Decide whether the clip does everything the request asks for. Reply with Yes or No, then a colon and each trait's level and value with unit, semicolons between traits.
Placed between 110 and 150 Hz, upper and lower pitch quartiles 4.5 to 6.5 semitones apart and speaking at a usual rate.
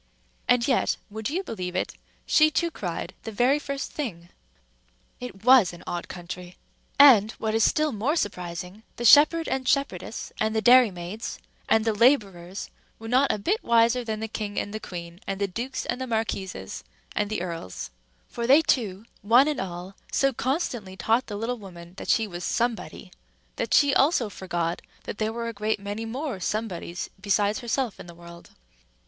No: high, 220 Hz; average, 4.9 semitones; average, 180 wpm